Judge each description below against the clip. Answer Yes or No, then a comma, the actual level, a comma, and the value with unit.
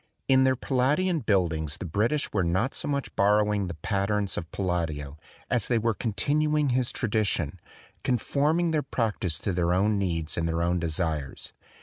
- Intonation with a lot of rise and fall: Yes, wide, 7.1 semitones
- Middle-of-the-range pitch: No, low, 100 Hz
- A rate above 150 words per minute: Yes, average, 175 wpm